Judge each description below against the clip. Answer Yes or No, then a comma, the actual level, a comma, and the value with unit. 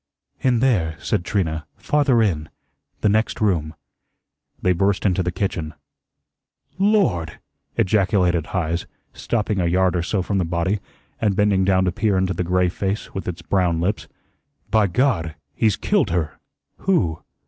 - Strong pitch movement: No, average, 3.5 semitones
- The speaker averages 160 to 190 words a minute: No, average, 150 wpm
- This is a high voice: No, very low, 95 Hz